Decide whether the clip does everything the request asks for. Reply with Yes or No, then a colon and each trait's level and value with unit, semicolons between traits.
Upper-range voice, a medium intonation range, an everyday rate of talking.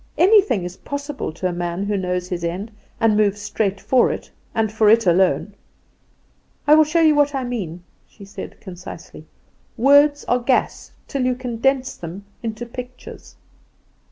No: high, 225 Hz; wide, 6.1 semitones; average, 160 wpm